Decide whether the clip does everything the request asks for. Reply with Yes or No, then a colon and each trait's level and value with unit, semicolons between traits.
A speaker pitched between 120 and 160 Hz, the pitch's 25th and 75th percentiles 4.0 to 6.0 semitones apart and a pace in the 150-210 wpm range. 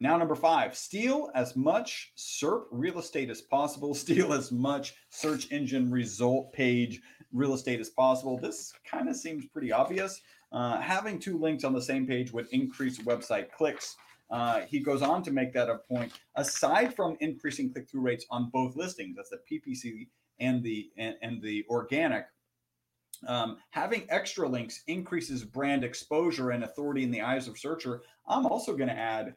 Yes: low, 135 Hz; wide, 5.4 semitones; average, 175 wpm